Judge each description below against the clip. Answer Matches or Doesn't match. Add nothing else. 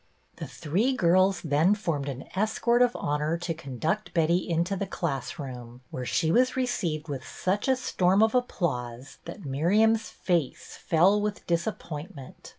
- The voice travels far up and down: Matches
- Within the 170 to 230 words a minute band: Doesn't match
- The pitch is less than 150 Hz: Doesn't match